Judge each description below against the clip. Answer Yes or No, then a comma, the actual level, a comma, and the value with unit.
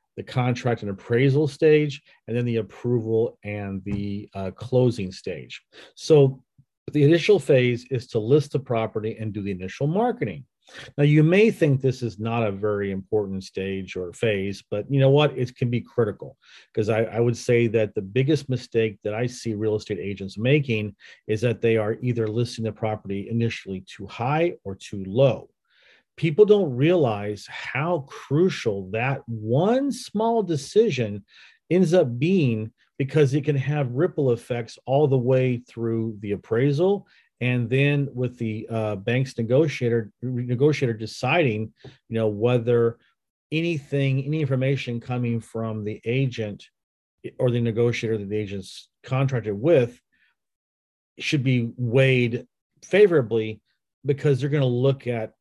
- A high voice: No, low, 120 Hz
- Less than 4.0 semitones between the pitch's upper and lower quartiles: No, average, 4.3 semitones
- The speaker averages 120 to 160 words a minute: Yes, average, 150 wpm